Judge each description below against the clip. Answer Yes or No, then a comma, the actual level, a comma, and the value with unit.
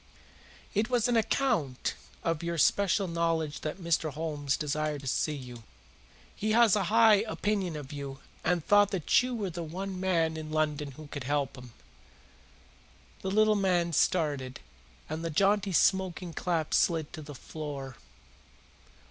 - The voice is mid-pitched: Yes, medium, 165 Hz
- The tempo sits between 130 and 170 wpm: Yes, average, 155 wpm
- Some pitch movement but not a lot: Yes, average, 4.8 semitones